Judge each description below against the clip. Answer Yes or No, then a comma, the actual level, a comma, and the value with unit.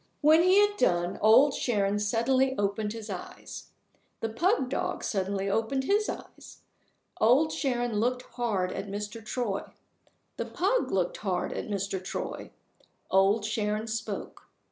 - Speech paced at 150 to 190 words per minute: No, average, 140 wpm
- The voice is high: Yes, high, 220 Hz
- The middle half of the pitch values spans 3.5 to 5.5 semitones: Yes, average, 4.7 semitones